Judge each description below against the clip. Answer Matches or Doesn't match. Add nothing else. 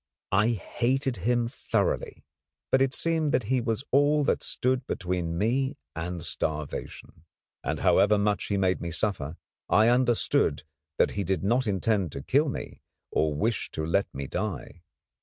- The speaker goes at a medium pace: Matches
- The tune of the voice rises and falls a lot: Matches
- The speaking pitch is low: Matches